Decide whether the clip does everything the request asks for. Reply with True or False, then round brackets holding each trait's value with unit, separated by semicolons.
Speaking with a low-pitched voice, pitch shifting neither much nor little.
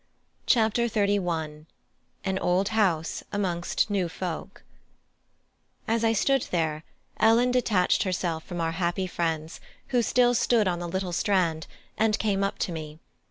False (185 Hz; 4.5 semitones)